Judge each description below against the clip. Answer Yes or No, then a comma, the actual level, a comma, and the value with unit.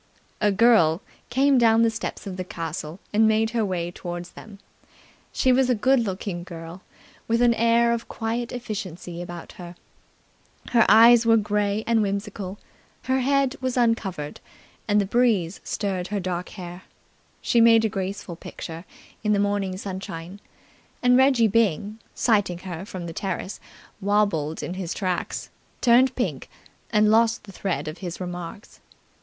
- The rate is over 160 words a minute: No, average, 155 wpm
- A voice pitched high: Yes, high, 205 Hz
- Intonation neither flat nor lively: Yes, average, 4.2 semitones